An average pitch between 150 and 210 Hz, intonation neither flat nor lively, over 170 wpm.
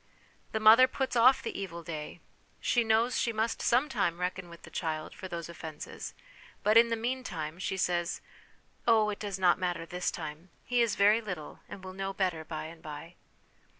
Yes: high, 190 Hz; average, 4.9 semitones; average, 190 wpm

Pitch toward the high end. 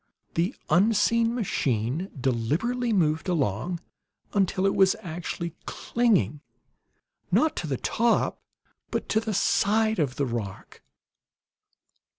No: medium, 180 Hz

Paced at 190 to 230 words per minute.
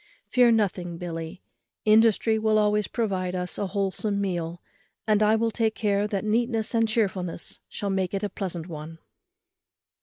No: average, 155 wpm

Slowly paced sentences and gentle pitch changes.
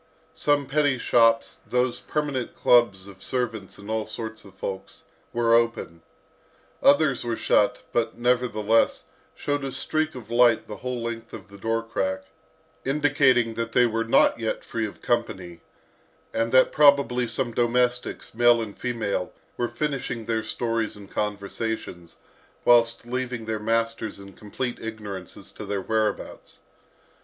No: average, 145 wpm; narrow, 2.3 semitones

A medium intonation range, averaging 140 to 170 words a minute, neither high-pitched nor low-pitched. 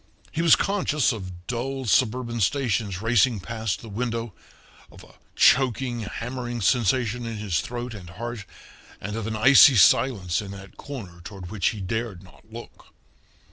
No: average, 3.7 semitones; average, 155 wpm; low, 115 Hz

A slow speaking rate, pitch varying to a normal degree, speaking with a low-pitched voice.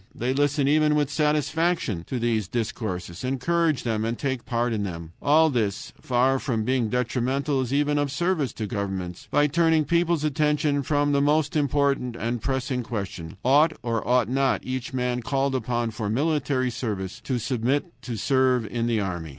No: average, 175 wpm; average, 4.0 semitones; low, 130 Hz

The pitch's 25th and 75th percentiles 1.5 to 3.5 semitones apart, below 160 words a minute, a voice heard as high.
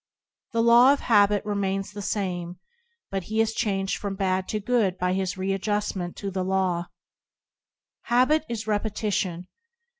Yes: narrow, 2.5 semitones; average, 150 wpm; high, 200 Hz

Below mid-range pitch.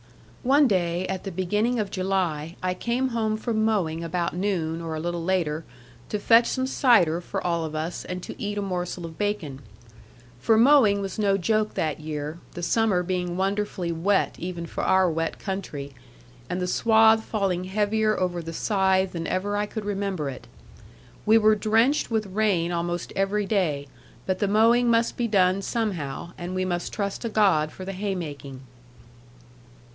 No: high, 190 Hz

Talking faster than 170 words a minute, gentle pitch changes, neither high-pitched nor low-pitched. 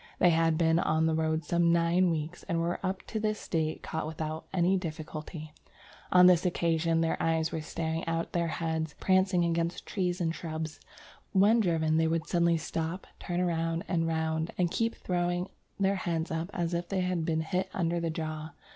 Yes: average, 200 wpm; narrow, 1.8 semitones; medium, 165 Hz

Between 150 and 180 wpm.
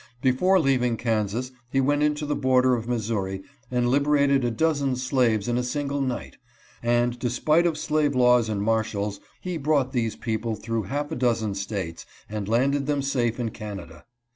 Yes: average, 170 wpm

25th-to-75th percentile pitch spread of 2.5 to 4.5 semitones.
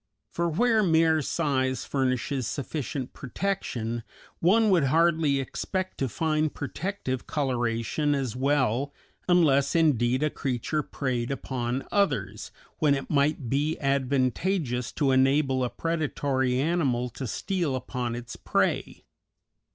Yes: average, 3.9 semitones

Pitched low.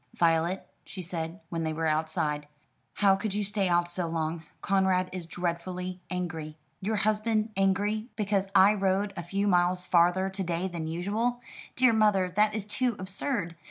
No: medium, 185 Hz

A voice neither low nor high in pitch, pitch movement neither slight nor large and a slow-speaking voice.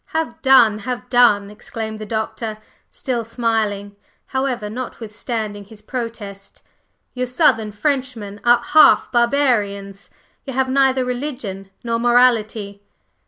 No: high, 230 Hz; average, 3.3 semitones; slow, 115 wpm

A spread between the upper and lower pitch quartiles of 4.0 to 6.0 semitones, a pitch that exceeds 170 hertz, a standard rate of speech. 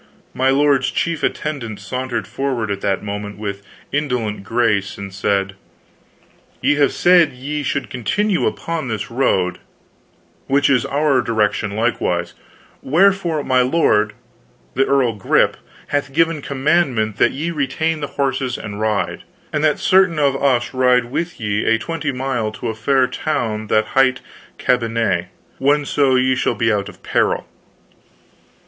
No: average, 4.9 semitones; low, 130 Hz; average, 145 wpm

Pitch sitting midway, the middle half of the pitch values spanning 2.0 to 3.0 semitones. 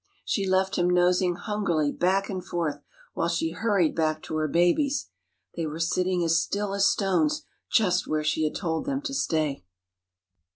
No: medium, 180 Hz; average, 3.4 semitones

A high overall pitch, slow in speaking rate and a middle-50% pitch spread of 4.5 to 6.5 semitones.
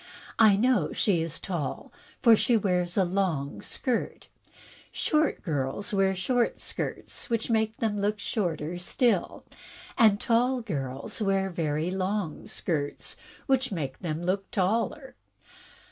Yes: high, 195 Hz; slow, 130 wpm; average, 4.8 semitones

